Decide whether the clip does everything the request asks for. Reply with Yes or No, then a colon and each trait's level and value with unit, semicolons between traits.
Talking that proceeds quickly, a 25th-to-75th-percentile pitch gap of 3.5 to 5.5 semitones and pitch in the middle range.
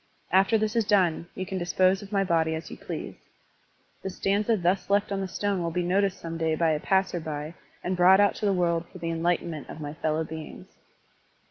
No: fast, 220 wpm; average, 3.0 semitones; medium, 180 Hz